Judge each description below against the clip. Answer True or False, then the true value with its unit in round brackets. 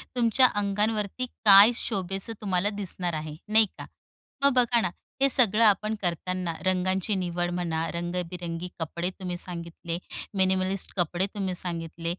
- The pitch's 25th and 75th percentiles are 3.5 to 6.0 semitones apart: False (3.0 semitones)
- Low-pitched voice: False (185 Hz)